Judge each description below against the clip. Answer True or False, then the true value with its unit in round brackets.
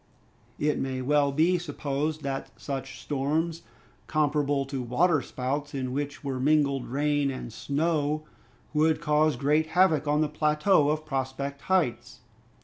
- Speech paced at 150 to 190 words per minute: False (140 wpm)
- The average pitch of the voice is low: False (145 Hz)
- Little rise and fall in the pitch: True (2.0 semitones)